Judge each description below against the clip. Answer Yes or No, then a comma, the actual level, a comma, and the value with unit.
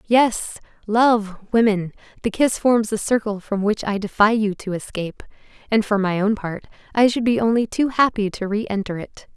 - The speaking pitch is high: Yes, high, 215 Hz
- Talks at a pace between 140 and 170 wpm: No, average, 185 wpm